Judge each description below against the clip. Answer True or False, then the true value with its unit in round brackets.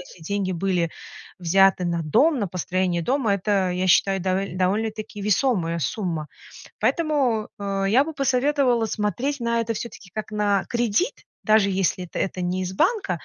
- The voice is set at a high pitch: True (200 Hz)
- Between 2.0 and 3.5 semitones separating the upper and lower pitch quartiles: False (4.2 semitones)